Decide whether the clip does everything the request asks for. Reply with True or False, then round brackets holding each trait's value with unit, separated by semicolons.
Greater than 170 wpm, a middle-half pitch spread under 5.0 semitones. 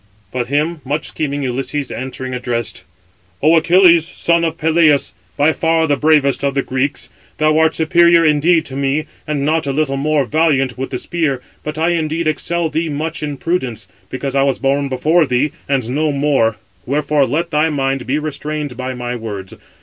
True (180 wpm; 2.9 semitones)